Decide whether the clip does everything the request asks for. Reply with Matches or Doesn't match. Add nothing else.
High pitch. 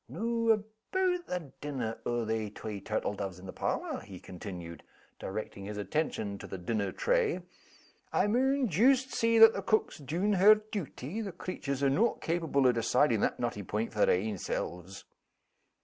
Doesn't match